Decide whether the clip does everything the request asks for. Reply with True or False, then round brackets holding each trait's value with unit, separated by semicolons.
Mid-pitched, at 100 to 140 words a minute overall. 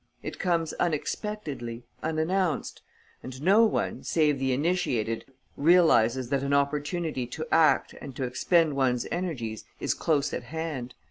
True (150 Hz; 135 wpm)